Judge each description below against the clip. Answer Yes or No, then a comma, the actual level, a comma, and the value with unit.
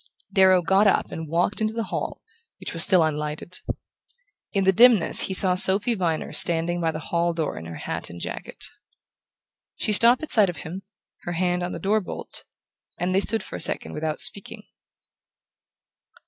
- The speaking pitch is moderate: Yes, medium, 180 Hz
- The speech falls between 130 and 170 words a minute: No, average, 180 wpm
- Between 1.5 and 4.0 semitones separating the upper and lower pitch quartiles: Yes, average, 3.5 semitones